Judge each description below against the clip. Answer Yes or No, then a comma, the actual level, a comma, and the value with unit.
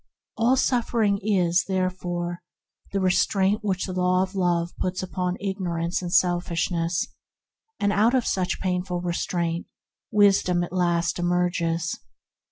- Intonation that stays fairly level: Yes, narrow, 1.9 semitones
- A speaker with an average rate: No, slow, 115 wpm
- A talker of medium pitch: Yes, medium, 180 Hz